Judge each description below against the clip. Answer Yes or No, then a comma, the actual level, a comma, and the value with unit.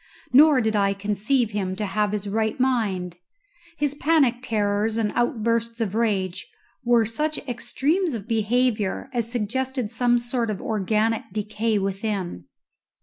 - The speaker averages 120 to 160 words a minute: Yes, average, 140 wpm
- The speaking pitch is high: Yes, high, 225 Hz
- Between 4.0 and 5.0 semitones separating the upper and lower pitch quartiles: No, average, 3.0 semitones